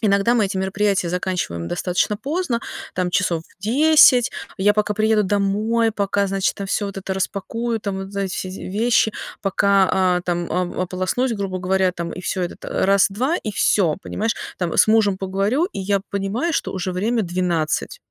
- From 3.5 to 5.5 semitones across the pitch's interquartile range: No, average, 2.7 semitones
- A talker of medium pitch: No, high, 195 Hz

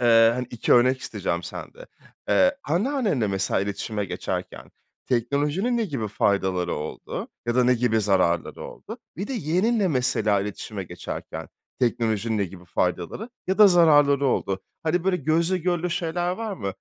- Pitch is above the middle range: No, low, 125 Hz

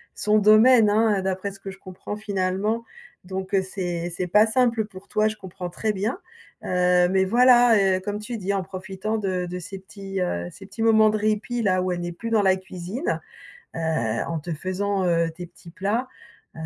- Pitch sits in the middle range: No, high, 195 Hz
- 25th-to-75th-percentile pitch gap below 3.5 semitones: Yes, average, 2.9 semitones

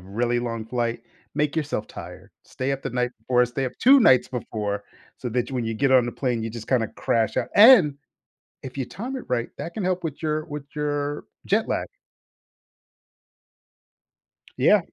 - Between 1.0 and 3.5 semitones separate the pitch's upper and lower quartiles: No, average, 4.1 semitones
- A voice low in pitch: Yes, low, 130 Hz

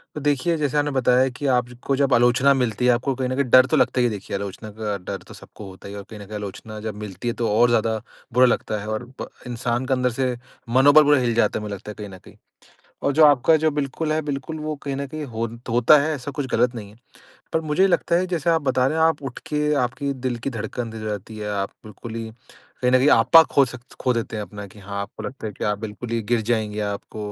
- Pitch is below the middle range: Yes, low, 125 Hz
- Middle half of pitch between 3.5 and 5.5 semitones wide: Yes, average, 4.5 semitones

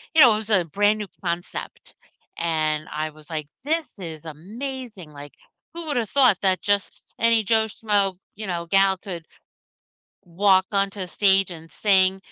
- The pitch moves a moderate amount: Yes, average, 4.1 semitones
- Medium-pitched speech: No, high, 195 Hz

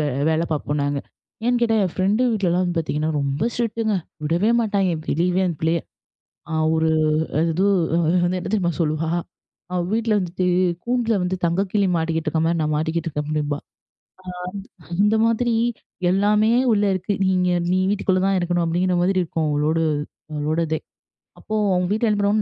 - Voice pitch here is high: No, medium, 180 Hz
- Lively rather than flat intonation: No, average, 4.2 semitones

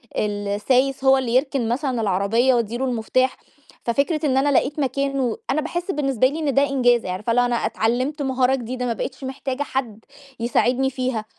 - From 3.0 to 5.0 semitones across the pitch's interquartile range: No, narrow, 2.6 semitones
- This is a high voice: Yes, very high, 255 Hz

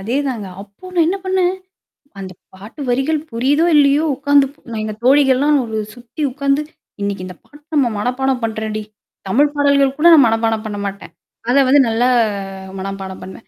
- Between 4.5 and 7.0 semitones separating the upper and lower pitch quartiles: Yes, average, 5.0 semitones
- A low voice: No, very high, 260 Hz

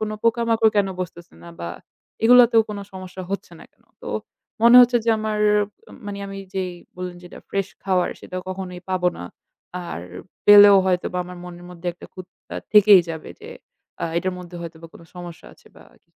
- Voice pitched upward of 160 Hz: Yes, medium, 185 Hz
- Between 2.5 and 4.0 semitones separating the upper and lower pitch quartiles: Yes, average, 2.8 semitones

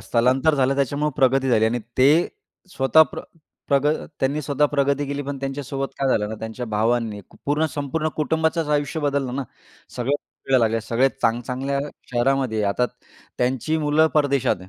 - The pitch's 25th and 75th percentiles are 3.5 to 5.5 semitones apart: No, average, 2.8 semitones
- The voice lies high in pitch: No, low, 135 Hz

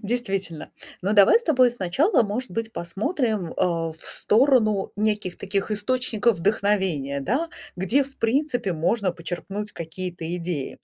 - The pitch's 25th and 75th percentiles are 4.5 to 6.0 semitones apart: Yes, average, 5.2 semitones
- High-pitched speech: Yes, high, 205 Hz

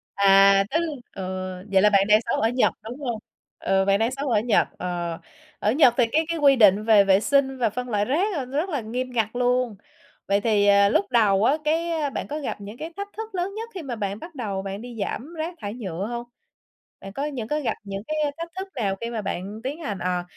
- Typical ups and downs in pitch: No, wide, 6.1 semitones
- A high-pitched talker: Yes, high, 230 Hz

